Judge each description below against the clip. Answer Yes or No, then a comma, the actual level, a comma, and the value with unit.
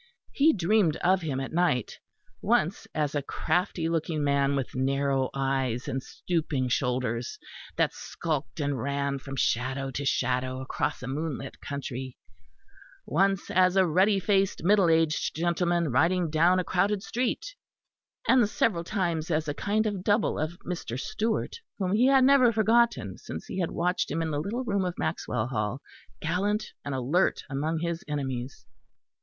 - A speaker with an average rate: Yes, average, 160 wpm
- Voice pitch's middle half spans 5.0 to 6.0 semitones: Yes, wide, 5.6 semitones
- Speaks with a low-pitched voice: No, medium, 160 Hz